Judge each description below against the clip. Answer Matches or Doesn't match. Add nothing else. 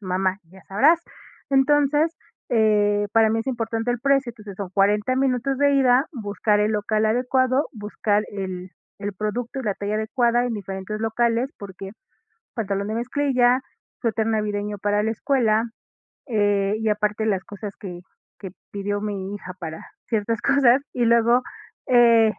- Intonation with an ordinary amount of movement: Matches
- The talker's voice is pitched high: Matches